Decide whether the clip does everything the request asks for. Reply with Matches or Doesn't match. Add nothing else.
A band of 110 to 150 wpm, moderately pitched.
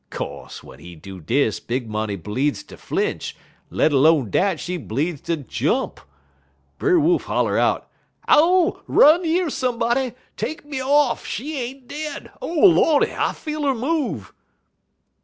Doesn't match